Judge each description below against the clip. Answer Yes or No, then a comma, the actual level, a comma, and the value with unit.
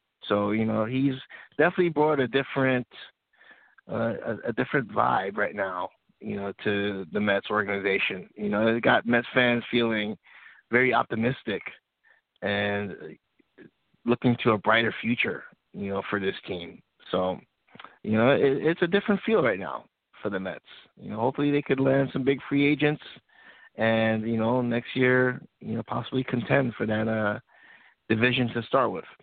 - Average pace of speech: Yes, average, 165 wpm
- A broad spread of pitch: No, average, 4.0 semitones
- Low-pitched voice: Yes, low, 120 Hz